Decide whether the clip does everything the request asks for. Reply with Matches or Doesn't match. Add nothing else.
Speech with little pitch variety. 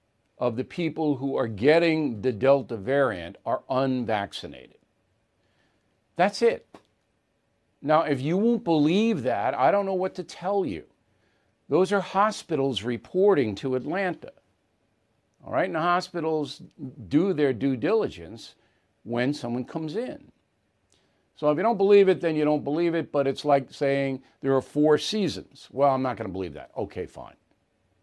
Doesn't match